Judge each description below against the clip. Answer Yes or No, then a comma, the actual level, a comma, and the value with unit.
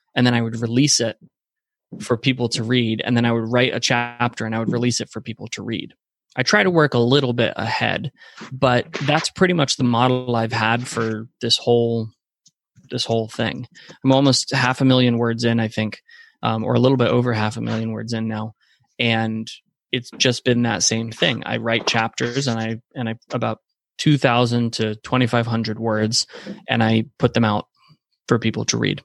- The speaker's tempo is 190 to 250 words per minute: Yes, average, 200 wpm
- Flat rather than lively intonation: Yes, narrow, 1.9 semitones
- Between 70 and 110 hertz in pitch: No, low, 120 Hz